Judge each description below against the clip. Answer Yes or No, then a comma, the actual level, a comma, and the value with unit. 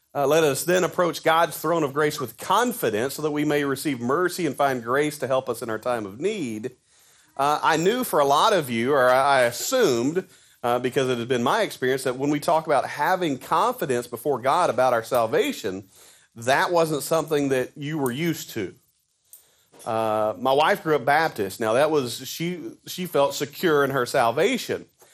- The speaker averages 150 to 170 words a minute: No, average, 195 wpm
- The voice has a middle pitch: Yes, medium, 145 Hz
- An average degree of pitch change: Yes, average, 4.0 semitones